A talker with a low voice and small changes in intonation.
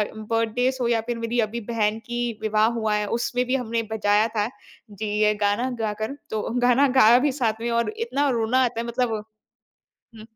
No: high, 230 Hz; narrow, 2.3 semitones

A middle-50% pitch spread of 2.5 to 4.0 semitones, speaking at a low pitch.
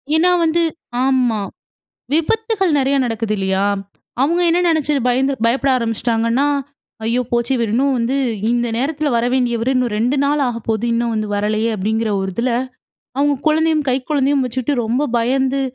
No: average, 3.7 semitones; very high, 250 Hz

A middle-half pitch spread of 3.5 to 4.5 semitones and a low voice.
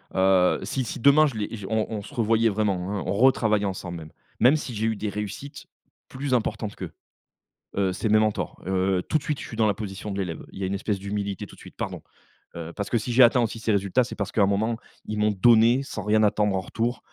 No: average, 2.9 semitones; low, 105 Hz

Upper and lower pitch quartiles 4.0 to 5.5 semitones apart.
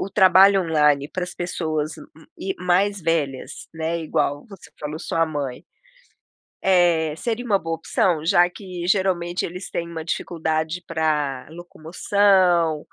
No: average, 2.7 semitones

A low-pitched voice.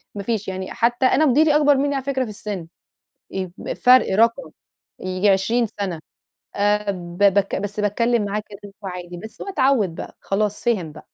No: high, 210 Hz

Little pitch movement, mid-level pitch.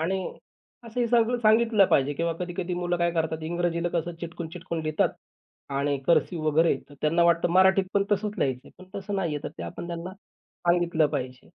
No: average, 3.0 semitones; medium, 170 Hz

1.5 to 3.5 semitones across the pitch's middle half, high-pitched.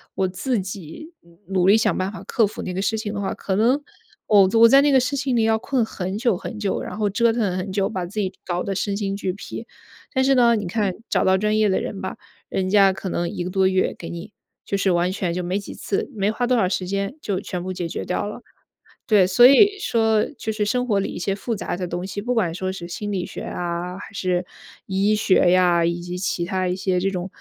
Yes: average, 3.1 semitones; high, 195 Hz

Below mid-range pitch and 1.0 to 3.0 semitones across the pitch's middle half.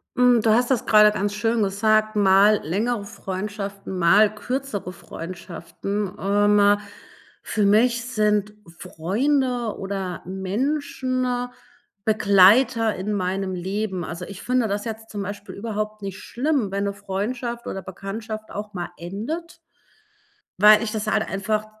No: high, 210 Hz; narrow, 2.6 semitones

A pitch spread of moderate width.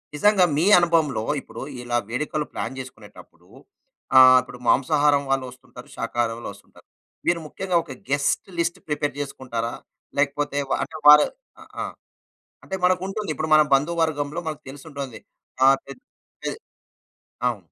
Yes: average, 3.5 semitones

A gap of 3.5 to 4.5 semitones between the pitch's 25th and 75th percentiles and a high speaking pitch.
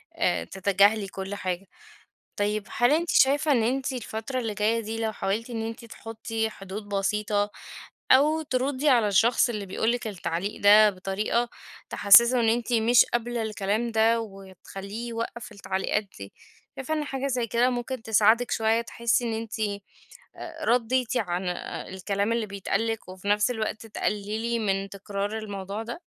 No: average, 2.8 semitones; high, 220 Hz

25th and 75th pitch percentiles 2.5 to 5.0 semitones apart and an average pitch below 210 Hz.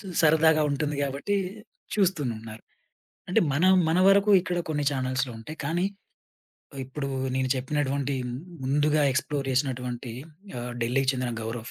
Yes: average, 3.4 semitones; medium, 140 Hz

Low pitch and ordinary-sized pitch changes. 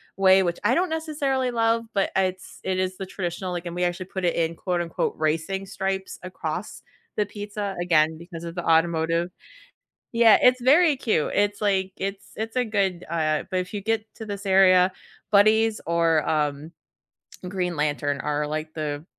No: medium, 185 Hz; average, 3.8 semitones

